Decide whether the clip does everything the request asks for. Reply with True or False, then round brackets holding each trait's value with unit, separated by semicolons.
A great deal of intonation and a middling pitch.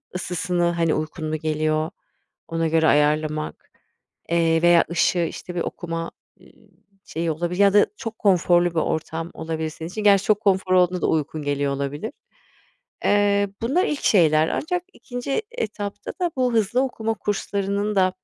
False (4.3 semitones; 175 Hz)